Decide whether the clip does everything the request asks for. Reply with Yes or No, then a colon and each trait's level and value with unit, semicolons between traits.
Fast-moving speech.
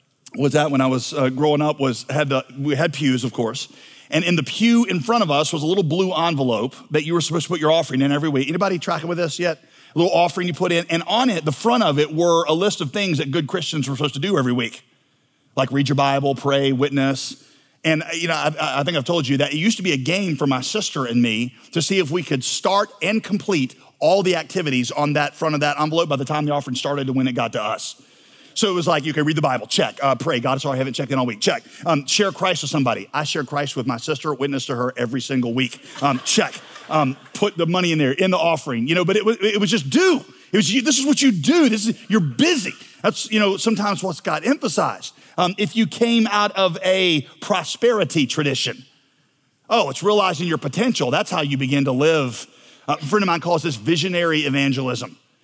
Yes: fast, 250 wpm